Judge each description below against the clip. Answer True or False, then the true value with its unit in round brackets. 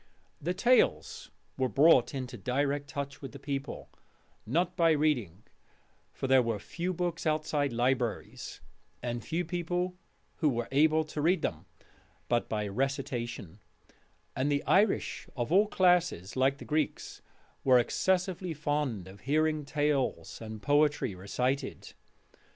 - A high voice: False (140 Hz)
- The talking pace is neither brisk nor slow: False (130 wpm)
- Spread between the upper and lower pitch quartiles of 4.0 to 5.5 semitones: True (4.5 semitones)